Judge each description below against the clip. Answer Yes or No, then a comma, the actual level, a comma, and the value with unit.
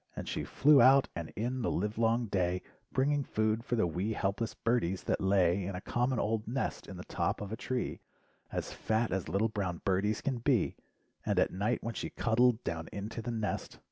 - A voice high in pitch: No, low, 110 Hz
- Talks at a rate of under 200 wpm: No, fast, 205 wpm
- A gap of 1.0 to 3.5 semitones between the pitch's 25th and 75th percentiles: No, average, 3.9 semitones